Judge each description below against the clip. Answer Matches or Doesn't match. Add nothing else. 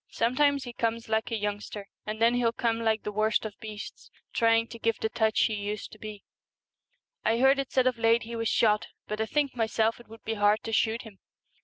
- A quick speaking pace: Matches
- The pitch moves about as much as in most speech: Doesn't match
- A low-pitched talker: Doesn't match